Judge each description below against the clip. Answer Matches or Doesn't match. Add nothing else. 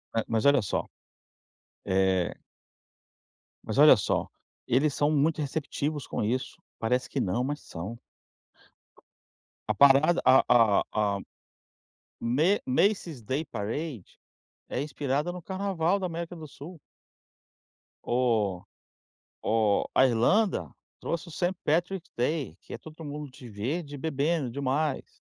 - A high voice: Doesn't match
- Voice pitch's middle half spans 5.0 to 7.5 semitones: Matches